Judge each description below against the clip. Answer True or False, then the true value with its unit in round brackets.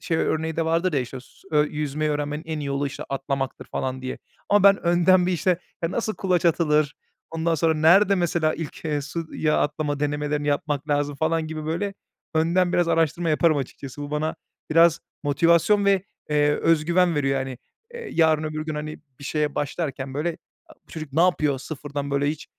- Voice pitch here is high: False (155 Hz)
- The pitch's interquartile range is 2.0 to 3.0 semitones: True (2.4 semitones)